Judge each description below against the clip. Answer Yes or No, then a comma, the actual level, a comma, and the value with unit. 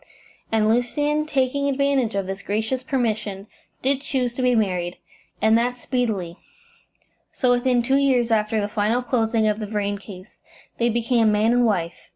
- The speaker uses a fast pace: No, average, 165 wpm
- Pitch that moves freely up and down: No, average, 3.2 semitones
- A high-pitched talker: Yes, high, 230 Hz